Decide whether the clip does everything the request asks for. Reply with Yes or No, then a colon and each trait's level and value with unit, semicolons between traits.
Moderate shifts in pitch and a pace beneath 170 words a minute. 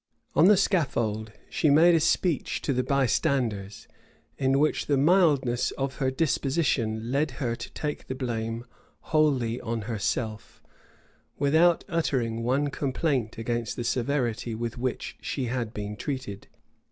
Yes: average, 4.1 semitones; average, 140 wpm